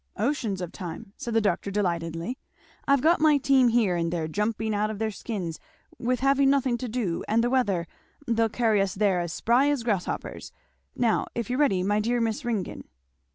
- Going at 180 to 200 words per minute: Yes, average, 195 wpm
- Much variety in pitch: No, average, 4.3 semitones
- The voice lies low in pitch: No, high, 220 Hz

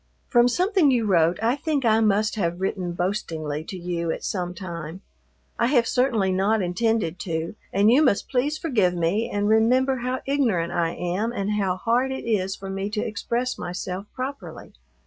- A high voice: Yes, high, 205 Hz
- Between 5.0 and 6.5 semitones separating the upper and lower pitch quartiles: Yes, average, 5.3 semitones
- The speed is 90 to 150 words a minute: No, average, 180 wpm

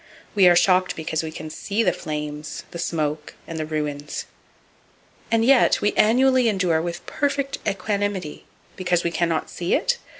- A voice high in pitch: No, medium, 175 Hz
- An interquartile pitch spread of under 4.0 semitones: No, average, 4.8 semitones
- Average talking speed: Yes, average, 165 wpm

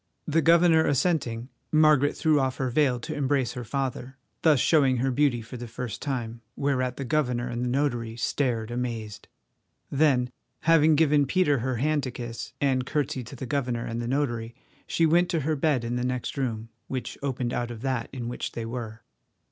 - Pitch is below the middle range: Yes, low, 130 Hz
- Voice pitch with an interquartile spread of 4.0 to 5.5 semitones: No, average, 3.4 semitones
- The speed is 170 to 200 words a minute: Yes, average, 190 wpm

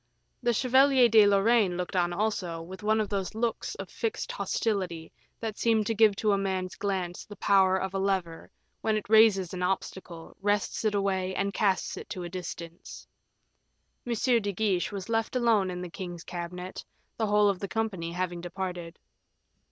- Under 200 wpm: Yes, average, 180 wpm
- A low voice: No, high, 195 Hz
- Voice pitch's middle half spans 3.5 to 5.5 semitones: No, average, 3.1 semitones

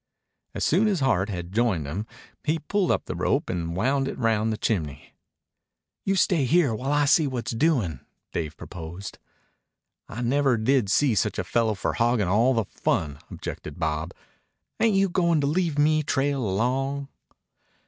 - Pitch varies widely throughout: Yes, wide, 7.0 semitones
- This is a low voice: Yes, low, 120 Hz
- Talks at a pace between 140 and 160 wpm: No, average, 170 wpm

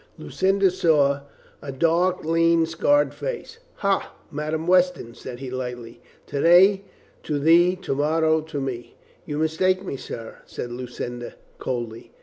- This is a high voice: No, medium, 160 Hz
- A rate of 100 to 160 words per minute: Yes, slow, 135 wpm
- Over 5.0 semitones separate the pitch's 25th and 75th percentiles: Yes, wide, 5.6 semitones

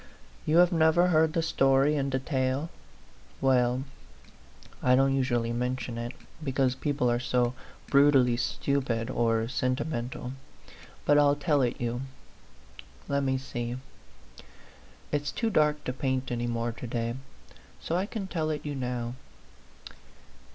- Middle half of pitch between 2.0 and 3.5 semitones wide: Yes, average, 3.2 semitones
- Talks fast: No, slow, 135 wpm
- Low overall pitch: Yes, low, 130 Hz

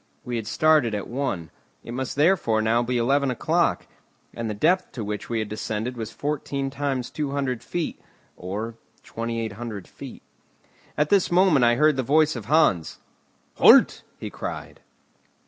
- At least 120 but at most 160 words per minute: Yes, average, 155 wpm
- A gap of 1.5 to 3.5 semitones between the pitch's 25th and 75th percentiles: No, average, 4.5 semitones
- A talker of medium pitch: No, low, 125 Hz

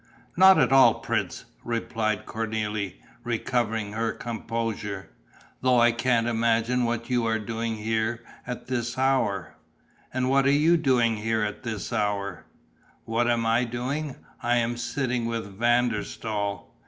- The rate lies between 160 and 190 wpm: No, average, 145 wpm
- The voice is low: Yes, low, 115 Hz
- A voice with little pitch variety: Yes, narrow, 1.9 semitones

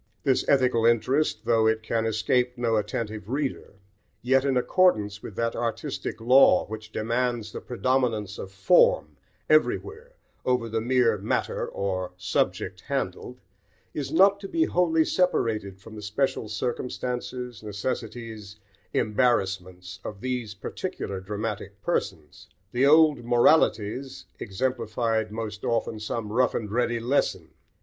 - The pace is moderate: No, slow, 125 wpm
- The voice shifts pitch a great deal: No, average, 3.3 semitones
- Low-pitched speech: Yes, low, 115 Hz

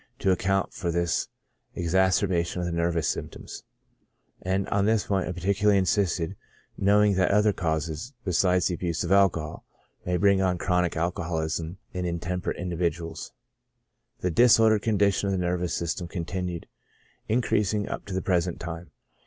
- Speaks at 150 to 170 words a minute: Yes, average, 155 wpm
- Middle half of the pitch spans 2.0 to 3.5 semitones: Yes, narrow, 2.4 semitones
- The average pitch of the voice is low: Yes, very low, 90 Hz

